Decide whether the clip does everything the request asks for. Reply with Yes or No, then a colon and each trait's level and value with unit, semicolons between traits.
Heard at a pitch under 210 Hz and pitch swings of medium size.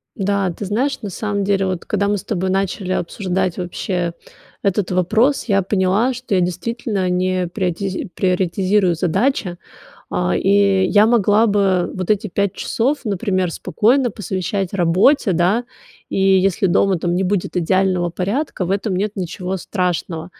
No: high, 190 Hz; narrow, 2.3 semitones